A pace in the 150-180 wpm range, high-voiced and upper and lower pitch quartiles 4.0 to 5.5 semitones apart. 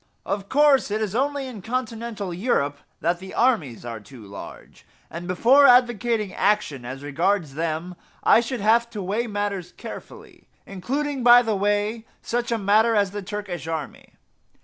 Yes: average, 160 wpm; high, 205 Hz; average, 5.2 semitones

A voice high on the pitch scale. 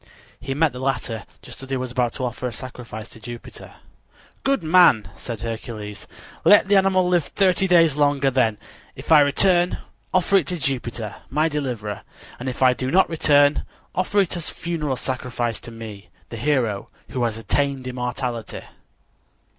No: low, 130 Hz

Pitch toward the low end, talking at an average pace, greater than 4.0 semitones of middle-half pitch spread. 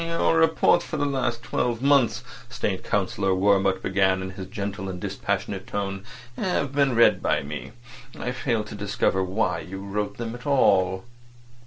Yes: low, 100 Hz; average, 165 wpm; average, 4.4 semitones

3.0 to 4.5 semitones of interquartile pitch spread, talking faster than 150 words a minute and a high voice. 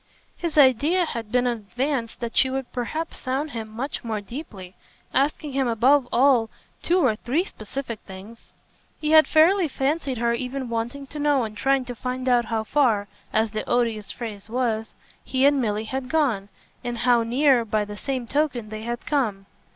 Yes: average, 3.7 semitones; average, 180 wpm; high, 245 Hz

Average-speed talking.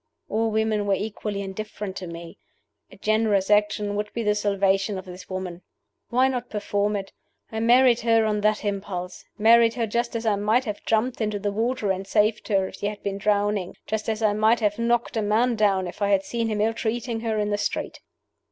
No: fast, 215 wpm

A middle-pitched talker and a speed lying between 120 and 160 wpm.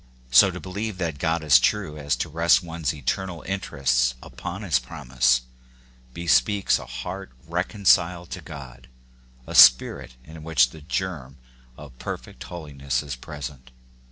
No: very low, 75 Hz; average, 140 wpm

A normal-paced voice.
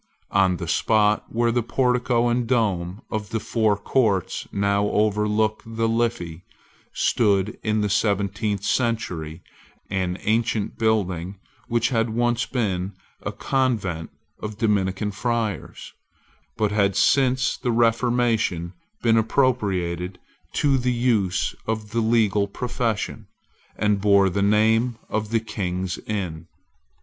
No: slow, 120 wpm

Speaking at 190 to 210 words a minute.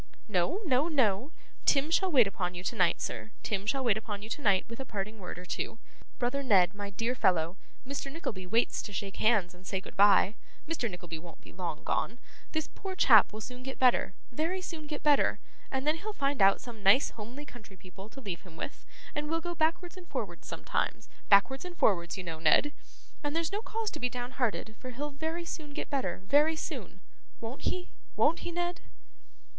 Yes: fast, 205 wpm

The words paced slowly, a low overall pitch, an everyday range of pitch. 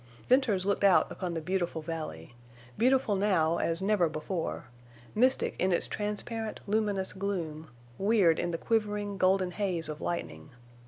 No: slow, 130 wpm; medium, 185 Hz; average, 4.1 semitones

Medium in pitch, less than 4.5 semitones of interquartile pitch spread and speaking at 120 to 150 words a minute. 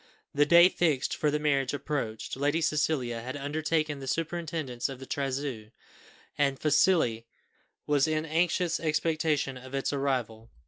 Yes: medium, 145 Hz; average, 2.9 semitones; average, 140 wpm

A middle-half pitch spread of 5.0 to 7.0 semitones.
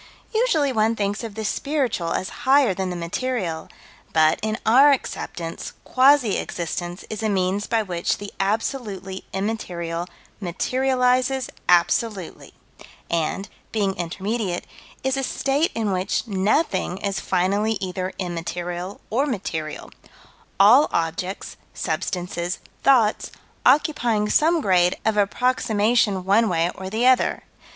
Yes: wide, 5.4 semitones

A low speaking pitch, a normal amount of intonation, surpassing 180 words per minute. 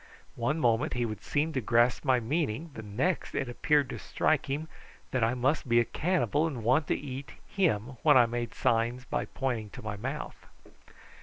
Yes: low, 125 Hz; average, 4.0 semitones; average, 190 wpm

